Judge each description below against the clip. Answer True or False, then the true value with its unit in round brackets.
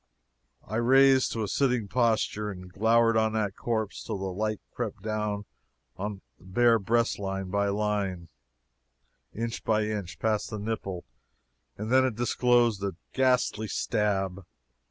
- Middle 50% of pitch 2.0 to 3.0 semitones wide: True (2.7 semitones)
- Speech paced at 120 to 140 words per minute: True (135 wpm)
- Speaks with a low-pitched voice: True (110 Hz)